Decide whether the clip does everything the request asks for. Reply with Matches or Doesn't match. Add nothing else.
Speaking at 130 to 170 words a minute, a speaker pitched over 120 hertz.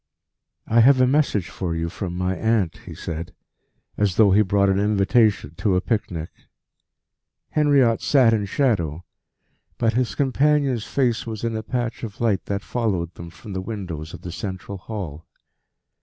Doesn't match